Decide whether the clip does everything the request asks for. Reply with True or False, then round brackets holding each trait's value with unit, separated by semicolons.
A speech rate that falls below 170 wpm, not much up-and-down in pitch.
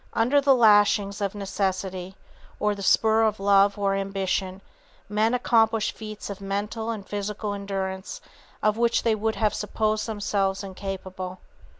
True (140 wpm; 1.9 semitones)